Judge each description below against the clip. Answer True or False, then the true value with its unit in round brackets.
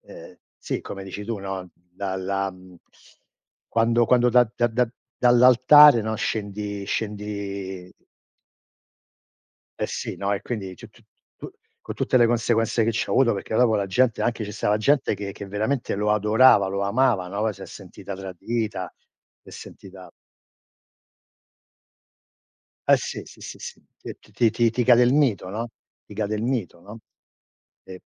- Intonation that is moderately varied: True (3.3 semitones)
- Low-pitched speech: True (105 Hz)